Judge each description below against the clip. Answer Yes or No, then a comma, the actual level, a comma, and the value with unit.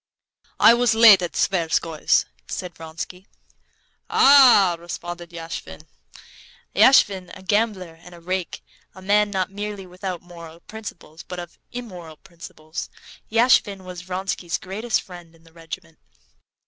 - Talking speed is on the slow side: Yes, slow, 130 wpm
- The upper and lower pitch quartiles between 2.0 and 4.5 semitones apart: Yes, average, 3.3 semitones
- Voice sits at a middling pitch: Yes, medium, 180 Hz